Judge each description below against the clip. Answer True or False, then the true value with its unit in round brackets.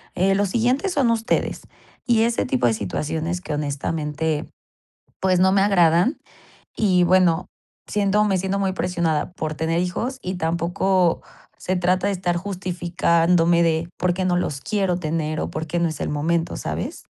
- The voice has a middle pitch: True (175 Hz)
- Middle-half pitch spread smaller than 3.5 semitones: True (2.9 semitones)